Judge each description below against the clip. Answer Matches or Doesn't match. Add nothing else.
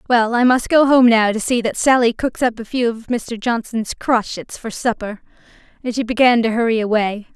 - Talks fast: Matches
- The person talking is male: Doesn't match